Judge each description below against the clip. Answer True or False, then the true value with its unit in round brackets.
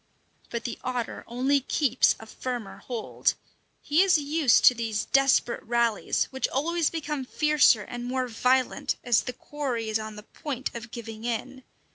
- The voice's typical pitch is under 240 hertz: False (250 Hz)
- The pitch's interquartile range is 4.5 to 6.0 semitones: False (3.2 semitones)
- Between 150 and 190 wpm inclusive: True (160 wpm)